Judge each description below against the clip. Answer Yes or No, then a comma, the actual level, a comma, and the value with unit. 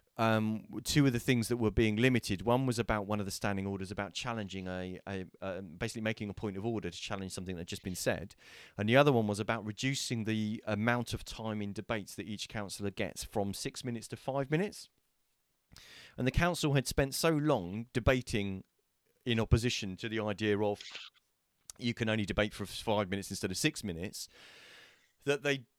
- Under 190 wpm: No, average, 200 wpm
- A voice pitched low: Yes, low, 110 Hz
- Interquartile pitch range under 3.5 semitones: Yes, average, 2.9 semitones